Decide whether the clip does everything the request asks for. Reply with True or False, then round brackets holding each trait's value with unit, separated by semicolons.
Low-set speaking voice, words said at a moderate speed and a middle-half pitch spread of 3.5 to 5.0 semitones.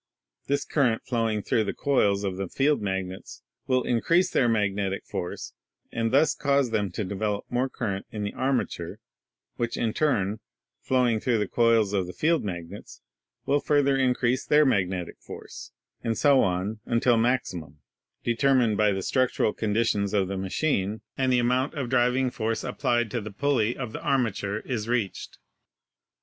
True (115 Hz; 160 wpm; 4.3 semitones)